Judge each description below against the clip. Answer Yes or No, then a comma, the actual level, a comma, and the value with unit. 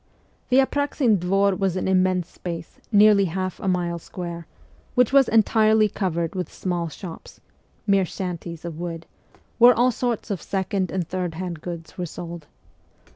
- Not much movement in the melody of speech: No, average, 3.2 semitones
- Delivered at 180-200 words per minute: No, average, 165 wpm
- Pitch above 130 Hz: Yes, medium, 185 Hz